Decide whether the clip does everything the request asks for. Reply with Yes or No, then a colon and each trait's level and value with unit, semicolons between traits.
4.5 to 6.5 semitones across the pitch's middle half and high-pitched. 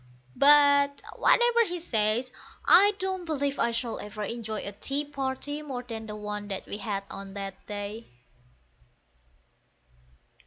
Yes: wide, 5.6 semitones; high, 240 Hz